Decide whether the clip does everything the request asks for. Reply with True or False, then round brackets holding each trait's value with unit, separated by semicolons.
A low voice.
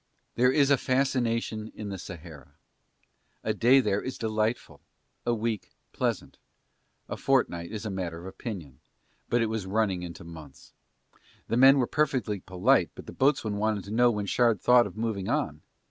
True (110 Hz)